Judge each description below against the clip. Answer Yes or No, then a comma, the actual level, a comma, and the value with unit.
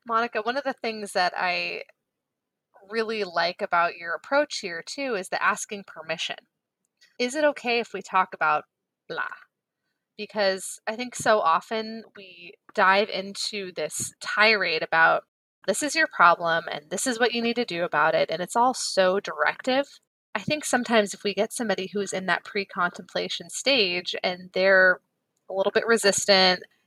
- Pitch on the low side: No, high, 200 Hz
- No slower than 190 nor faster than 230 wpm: No, average, 165 wpm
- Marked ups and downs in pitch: No, average, 4.4 semitones